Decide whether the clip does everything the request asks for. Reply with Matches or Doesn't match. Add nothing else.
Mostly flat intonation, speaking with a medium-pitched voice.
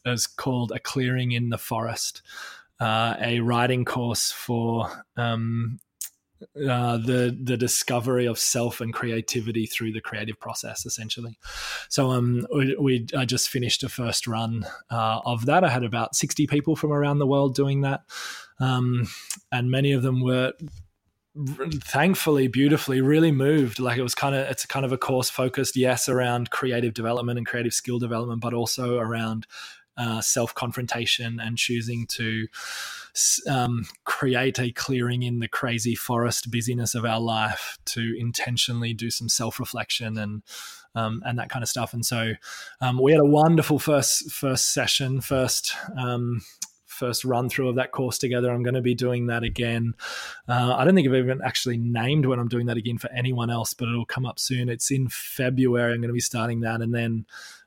Doesn't match